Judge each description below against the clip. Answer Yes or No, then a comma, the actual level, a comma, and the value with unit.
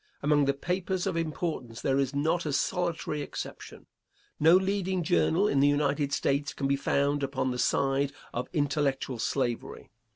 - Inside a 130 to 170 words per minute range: Yes, average, 160 wpm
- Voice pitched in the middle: Yes, medium, 145 Hz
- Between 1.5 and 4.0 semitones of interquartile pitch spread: Yes, average, 3.3 semitones